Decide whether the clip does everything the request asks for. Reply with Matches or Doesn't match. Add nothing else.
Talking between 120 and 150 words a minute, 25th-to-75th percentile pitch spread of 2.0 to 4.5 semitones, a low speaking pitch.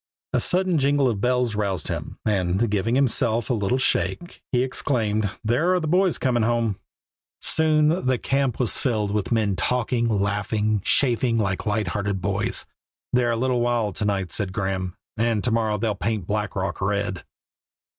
Doesn't match